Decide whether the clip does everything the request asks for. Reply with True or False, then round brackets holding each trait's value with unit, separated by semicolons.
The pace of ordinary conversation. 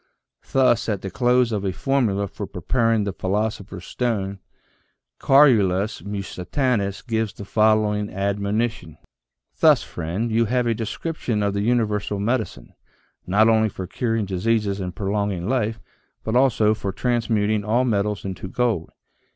True (145 wpm)